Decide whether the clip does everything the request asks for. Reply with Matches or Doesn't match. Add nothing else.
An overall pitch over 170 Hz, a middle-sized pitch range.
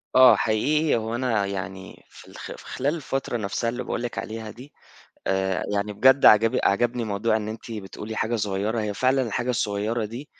Doesn't match